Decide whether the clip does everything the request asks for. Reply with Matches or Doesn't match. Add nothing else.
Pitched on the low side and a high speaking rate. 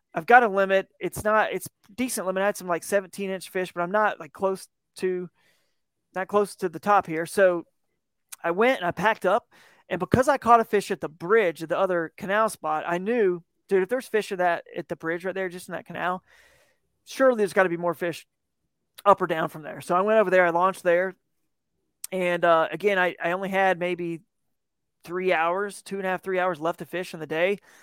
Doesn't match